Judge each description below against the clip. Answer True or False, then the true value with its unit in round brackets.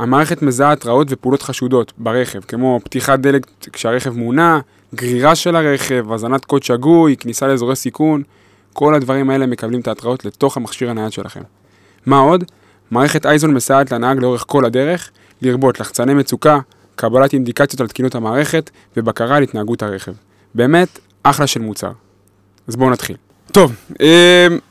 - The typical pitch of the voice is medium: False (130 Hz)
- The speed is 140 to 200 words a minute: True (150 wpm)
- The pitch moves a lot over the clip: False (3.6 semitones)